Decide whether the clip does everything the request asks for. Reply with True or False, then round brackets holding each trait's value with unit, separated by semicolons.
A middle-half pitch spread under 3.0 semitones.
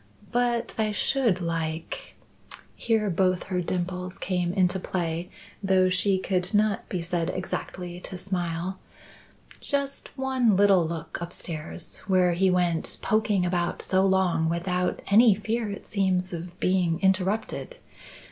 True (2.4 semitones)